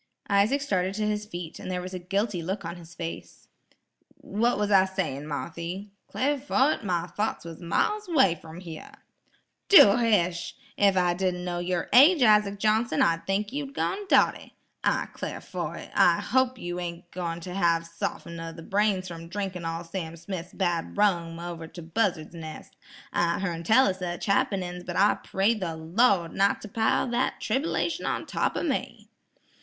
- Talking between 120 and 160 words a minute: No, average, 180 wpm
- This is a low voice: No, medium, 185 Hz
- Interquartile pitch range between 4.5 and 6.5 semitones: No, average, 3.6 semitones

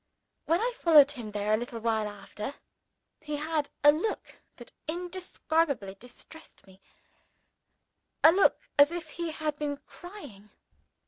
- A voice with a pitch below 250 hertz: No, very high, 295 Hz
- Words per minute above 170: No, slow, 135 wpm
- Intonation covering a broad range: Yes, wide, 6.9 semitones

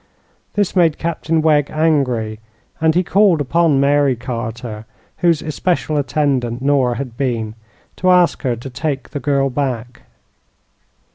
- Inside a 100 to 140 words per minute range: Yes, slow, 135 wpm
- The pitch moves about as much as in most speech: Yes, average, 4.4 semitones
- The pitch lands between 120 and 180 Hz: Yes, medium, 140 Hz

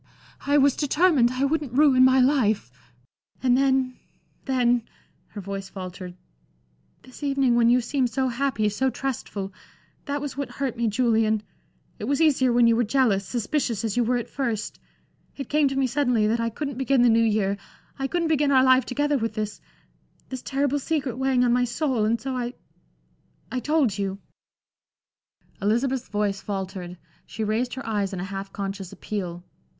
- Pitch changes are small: No, average, 4.2 semitones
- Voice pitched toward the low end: No, high, 245 Hz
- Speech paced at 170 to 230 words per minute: Yes, average, 175 wpm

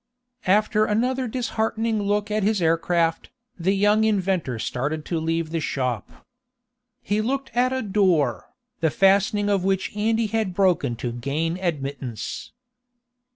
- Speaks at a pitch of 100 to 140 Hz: No, high, 195 Hz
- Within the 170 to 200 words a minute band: No, average, 140 wpm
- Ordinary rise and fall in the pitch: Yes, average, 5.0 semitones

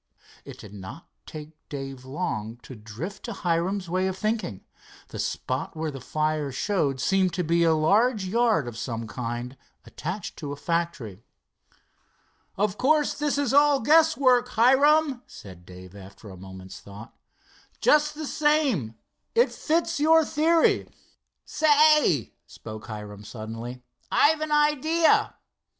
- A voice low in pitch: No, medium, 170 Hz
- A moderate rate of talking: Yes, average, 145 wpm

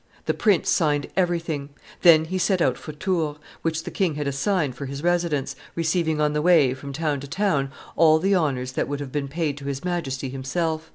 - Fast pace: Yes, fast, 210 wpm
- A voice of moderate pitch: Yes, medium, 155 Hz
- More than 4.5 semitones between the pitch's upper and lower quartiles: No, average, 3.5 semitones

